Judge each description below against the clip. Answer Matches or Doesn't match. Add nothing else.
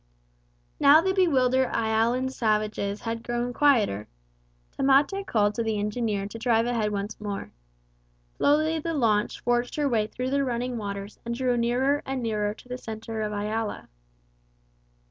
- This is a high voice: Matches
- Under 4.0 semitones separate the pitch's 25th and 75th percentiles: Matches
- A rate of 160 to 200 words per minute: Doesn't match